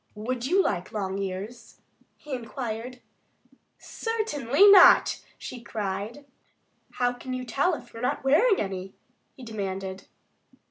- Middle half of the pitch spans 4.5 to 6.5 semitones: Yes, average, 5.0 semitones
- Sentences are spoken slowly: Yes, slow, 130 wpm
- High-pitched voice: Yes, high, 240 Hz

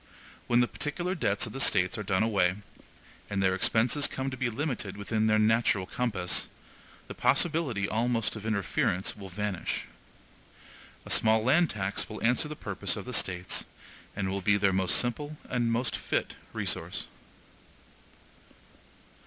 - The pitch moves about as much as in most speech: Yes, average, 4.0 semitones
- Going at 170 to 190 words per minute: No, average, 155 wpm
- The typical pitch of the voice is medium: No, low, 110 Hz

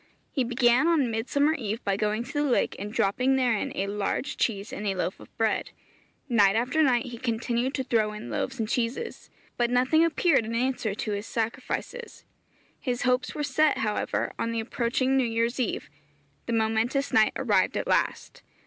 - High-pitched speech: Yes, high, 240 Hz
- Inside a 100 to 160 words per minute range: No, average, 185 wpm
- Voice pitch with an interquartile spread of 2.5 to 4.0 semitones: Yes, average, 3.1 semitones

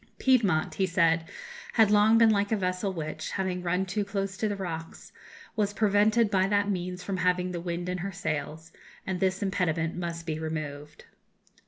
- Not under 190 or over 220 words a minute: No, average, 180 wpm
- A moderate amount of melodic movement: Yes, average, 3.2 semitones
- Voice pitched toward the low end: No, medium, 185 Hz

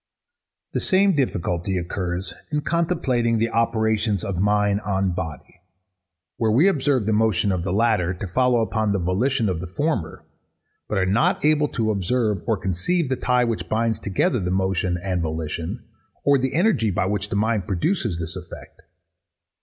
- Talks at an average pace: Yes, average, 170 wpm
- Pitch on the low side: Yes, low, 105 Hz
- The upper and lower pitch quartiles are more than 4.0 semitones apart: Yes, average, 5.1 semitones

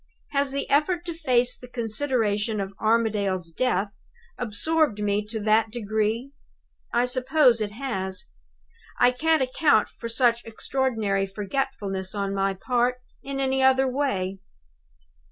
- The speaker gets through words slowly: Yes, slow, 130 wpm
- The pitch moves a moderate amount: Yes, average, 4.4 semitones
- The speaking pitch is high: Yes, high, 235 Hz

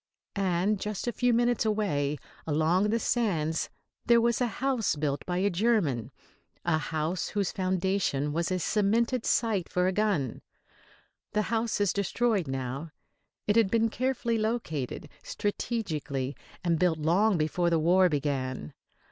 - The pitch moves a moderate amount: No, wide, 5.9 semitones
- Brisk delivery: No, average, 145 wpm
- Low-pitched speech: No, medium, 185 Hz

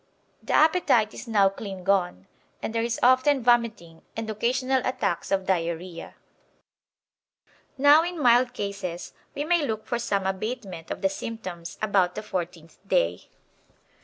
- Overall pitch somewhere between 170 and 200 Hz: No, high, 210 Hz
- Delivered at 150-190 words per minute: No, average, 140 wpm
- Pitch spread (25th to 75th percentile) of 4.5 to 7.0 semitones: Yes, average, 5.0 semitones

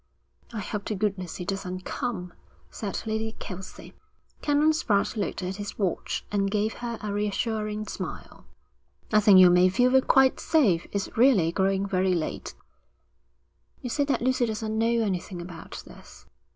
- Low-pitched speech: No, high, 210 Hz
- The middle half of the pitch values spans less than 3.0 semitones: No, average, 3.5 semitones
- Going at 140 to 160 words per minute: Yes, average, 155 wpm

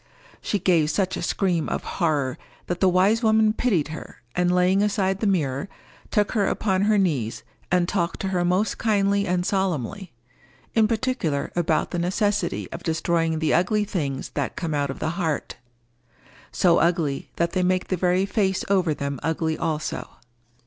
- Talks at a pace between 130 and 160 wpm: No, average, 170 wpm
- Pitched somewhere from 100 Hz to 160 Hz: No, medium, 180 Hz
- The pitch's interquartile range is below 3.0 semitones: No, average, 3.8 semitones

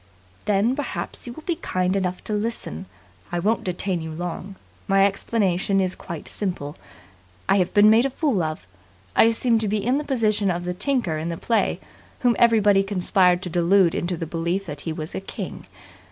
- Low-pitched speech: No, high, 195 Hz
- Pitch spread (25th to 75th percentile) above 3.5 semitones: Yes, average, 4.1 semitones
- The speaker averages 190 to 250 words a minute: Yes, average, 195 wpm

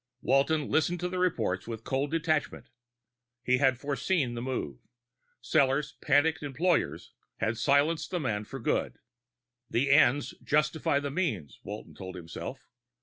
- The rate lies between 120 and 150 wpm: Yes, average, 140 wpm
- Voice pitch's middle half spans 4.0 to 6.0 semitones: Yes, average, 4.6 semitones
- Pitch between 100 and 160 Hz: Yes, medium, 140 Hz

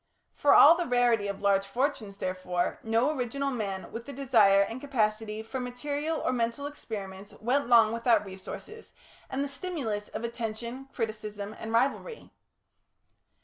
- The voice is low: No, high, 230 Hz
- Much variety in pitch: No, average, 4.4 semitones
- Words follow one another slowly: No, average, 145 wpm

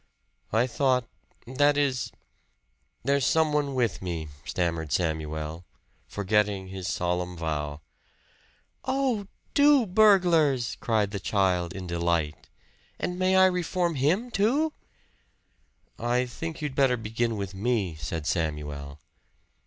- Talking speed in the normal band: No, slow, 115 wpm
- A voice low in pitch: Yes, low, 115 Hz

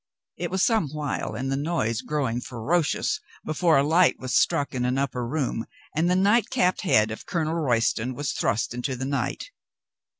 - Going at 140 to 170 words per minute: No, average, 190 wpm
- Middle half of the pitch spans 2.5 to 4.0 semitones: No, average, 5.3 semitones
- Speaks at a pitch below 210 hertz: Yes, medium, 140 Hz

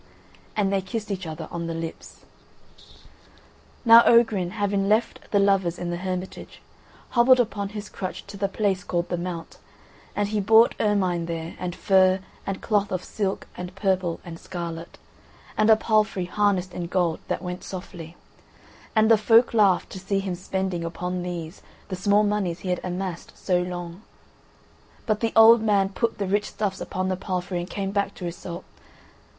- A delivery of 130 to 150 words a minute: No, average, 175 wpm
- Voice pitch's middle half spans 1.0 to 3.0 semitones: Yes, narrow, 2.6 semitones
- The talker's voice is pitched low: No, high, 190 Hz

